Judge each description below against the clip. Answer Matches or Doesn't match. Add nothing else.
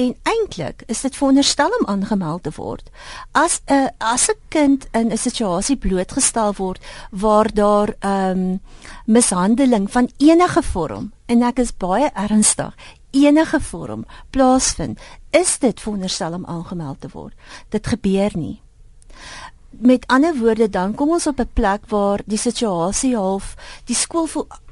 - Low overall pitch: Doesn't match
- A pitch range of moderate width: Doesn't match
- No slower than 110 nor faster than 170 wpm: Matches